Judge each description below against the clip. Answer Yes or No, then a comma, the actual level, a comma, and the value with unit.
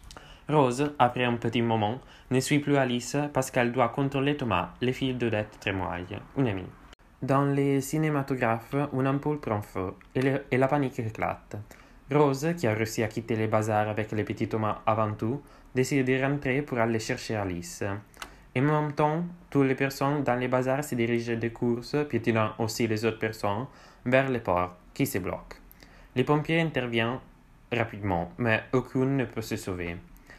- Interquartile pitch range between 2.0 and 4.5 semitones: Yes, average, 3.8 semitones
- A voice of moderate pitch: No, low, 120 Hz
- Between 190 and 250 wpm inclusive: No, average, 175 wpm